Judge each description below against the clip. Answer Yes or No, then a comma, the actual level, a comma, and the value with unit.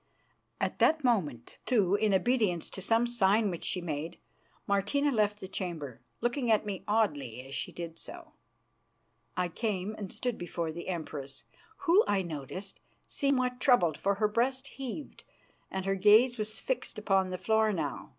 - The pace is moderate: Yes, average, 165 wpm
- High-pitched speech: Yes, high, 205 Hz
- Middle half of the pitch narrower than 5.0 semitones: No, wide, 5.4 semitones